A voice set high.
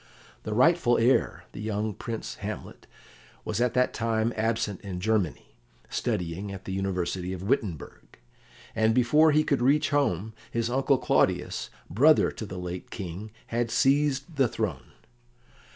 No: low, 110 Hz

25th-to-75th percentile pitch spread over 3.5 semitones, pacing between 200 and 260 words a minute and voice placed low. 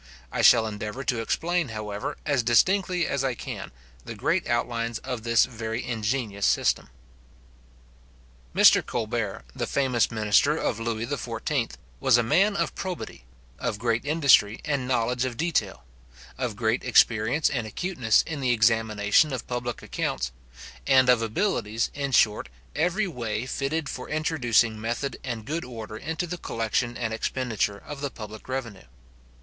No: average, 3.9 semitones; average, 150 wpm; low, 120 Hz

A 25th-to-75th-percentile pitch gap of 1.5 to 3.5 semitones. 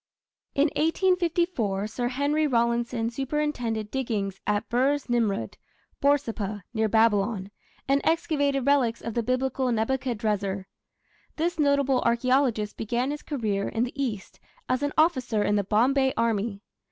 No: average, 4.4 semitones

